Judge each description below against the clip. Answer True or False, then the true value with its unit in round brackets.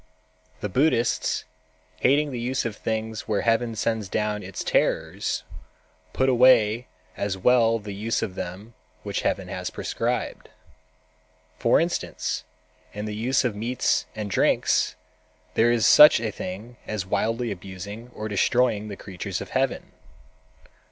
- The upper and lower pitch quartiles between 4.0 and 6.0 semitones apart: False (2.9 semitones)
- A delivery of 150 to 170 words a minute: False (140 wpm)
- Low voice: True (110 Hz)